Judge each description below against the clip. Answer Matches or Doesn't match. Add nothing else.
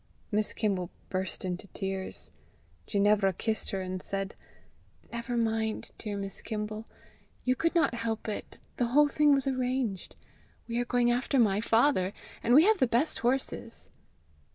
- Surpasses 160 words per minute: Doesn't match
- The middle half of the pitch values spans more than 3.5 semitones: Matches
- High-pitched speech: Matches